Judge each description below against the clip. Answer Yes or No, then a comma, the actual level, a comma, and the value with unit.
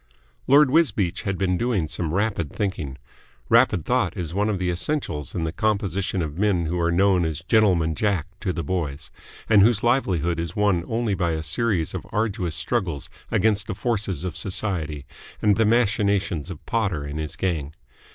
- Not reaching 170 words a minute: No, average, 180 wpm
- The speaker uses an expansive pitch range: No, average, 4.4 semitones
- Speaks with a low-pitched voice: Yes, very low, 95 Hz